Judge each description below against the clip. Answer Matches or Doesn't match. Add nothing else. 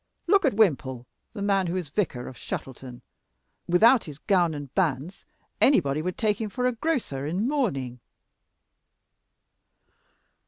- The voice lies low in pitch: Doesn't match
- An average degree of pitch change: Doesn't match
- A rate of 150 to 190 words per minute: Doesn't match